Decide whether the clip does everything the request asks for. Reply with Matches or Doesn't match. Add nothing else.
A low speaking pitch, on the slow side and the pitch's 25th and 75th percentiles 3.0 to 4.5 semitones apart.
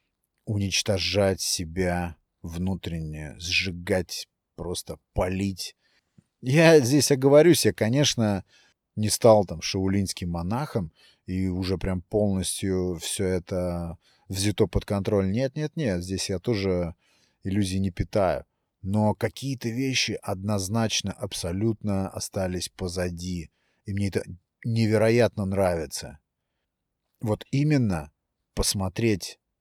Matches